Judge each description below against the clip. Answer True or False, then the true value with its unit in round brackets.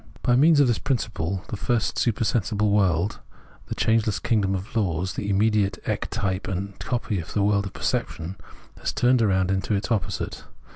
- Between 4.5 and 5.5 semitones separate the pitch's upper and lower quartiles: False (2.9 semitones)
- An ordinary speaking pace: True (165 wpm)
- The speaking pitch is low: True (100 Hz)